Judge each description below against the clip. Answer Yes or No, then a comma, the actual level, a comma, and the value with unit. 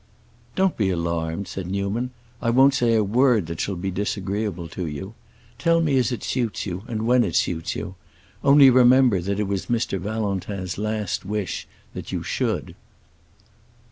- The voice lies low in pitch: Yes, low, 105 Hz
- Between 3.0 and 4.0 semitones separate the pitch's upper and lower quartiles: No, average, 4.5 semitones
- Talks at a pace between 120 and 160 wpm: No, average, 170 wpm